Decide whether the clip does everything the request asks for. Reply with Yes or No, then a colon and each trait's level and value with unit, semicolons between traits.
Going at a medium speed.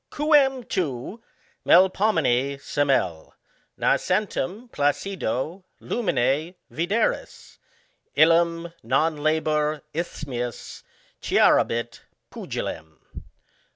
No: slow, 65 wpm